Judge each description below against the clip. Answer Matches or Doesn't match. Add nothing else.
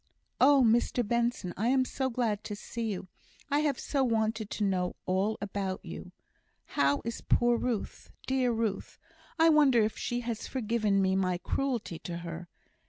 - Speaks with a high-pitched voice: Matches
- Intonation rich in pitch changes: Doesn't match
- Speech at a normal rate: Matches